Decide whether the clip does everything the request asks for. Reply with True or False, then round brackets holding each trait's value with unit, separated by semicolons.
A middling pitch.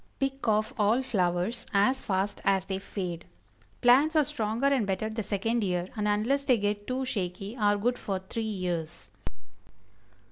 False (210 Hz)